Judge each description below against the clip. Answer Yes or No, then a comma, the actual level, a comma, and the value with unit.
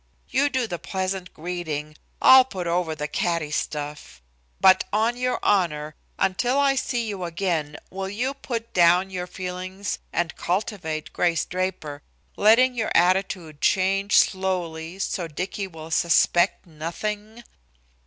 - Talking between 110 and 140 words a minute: Yes, slow, 135 wpm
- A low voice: No, medium, 185 Hz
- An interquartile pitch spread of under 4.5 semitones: Yes, average, 3.8 semitones